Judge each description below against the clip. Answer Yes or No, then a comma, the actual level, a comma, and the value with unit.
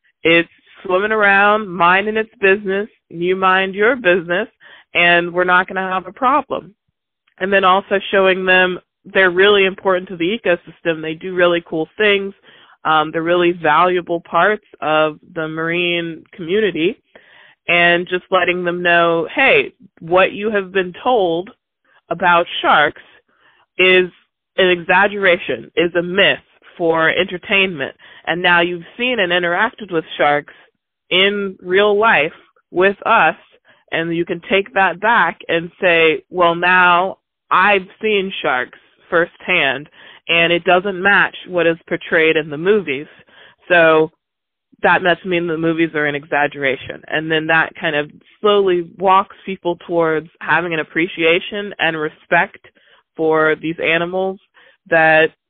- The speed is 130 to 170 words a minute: Yes, average, 140 wpm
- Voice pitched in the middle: Yes, medium, 180 Hz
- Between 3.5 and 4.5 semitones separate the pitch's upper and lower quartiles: No, narrow, 2.6 semitones